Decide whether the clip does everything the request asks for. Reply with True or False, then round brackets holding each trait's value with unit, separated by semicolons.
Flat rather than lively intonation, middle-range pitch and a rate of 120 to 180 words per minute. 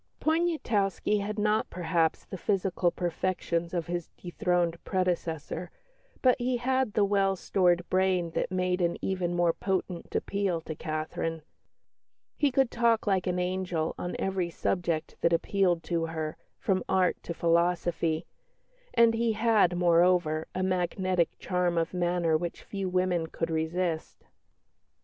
True (2.3 semitones; 180 Hz; 140 wpm)